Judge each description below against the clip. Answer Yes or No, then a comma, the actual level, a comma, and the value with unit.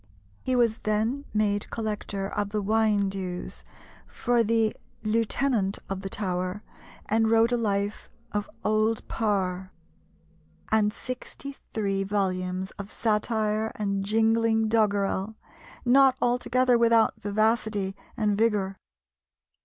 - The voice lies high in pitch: Yes, high, 215 Hz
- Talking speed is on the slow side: Yes, slow, 115 wpm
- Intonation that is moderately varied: No, narrow, 2.3 semitones